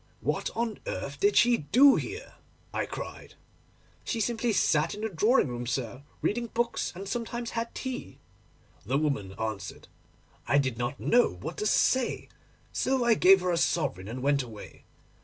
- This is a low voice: No, high, 195 Hz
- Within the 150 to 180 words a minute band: Yes, average, 165 wpm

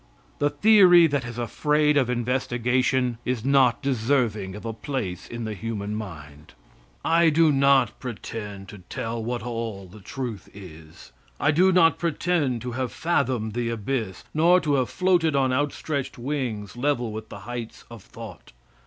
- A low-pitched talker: Yes, low, 120 Hz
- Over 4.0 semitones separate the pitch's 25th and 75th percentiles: Yes, average, 4.6 semitones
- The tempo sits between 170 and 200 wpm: No, average, 160 wpm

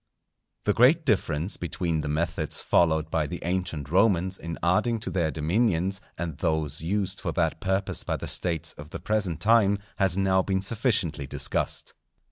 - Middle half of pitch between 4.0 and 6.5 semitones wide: No, average, 3.5 semitones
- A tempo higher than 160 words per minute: Yes, average, 170 wpm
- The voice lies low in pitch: Yes, very low, 90 Hz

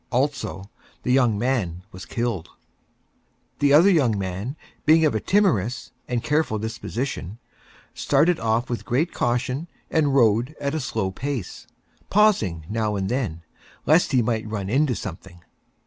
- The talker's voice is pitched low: Yes, low, 120 Hz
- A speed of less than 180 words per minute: Yes, average, 145 wpm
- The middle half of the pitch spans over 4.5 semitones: Yes, wide, 5.5 semitones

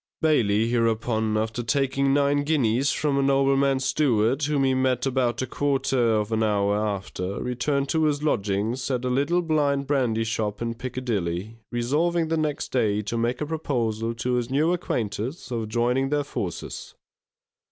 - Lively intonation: No, average, 3.9 semitones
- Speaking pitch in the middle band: No, low, 125 Hz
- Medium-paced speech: Yes, average, 165 wpm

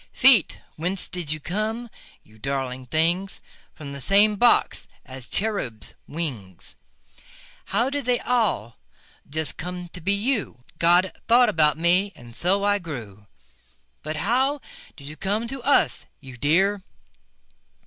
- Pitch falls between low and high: Yes, medium, 175 Hz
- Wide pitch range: Yes, wide, 7.0 semitones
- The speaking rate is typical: No, slow, 130 wpm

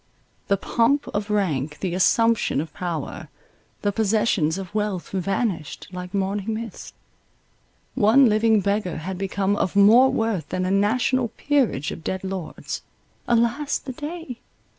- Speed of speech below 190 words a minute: Yes, average, 140 wpm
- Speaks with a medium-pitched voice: No, high, 205 Hz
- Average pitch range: Yes, average, 3.7 semitones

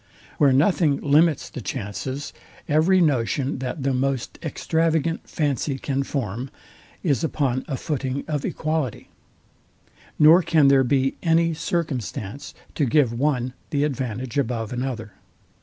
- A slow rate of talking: Yes, slow, 125 wpm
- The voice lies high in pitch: No, medium, 140 Hz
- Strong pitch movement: No, average, 3.3 semitones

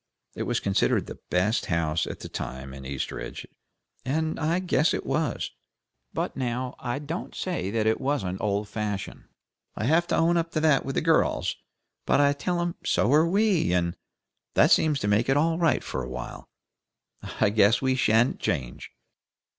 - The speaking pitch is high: No, low, 130 Hz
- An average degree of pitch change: No, wide, 8.0 semitones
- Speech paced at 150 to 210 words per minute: Yes, average, 180 wpm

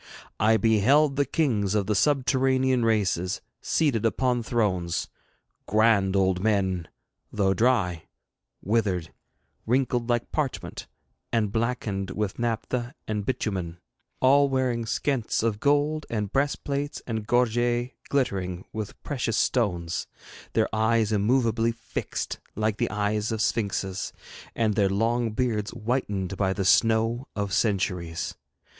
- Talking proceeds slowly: Yes, slow, 120 wpm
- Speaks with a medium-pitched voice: No, low, 110 Hz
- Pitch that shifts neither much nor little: Yes, average, 3.7 semitones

